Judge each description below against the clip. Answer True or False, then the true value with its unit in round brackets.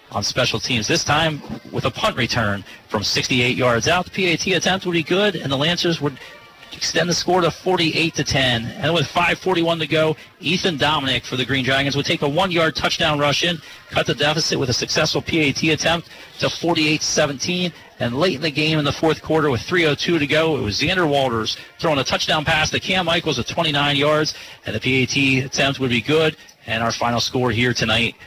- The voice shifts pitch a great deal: False (4.4 semitones)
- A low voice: False (150 Hz)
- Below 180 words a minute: False (205 wpm)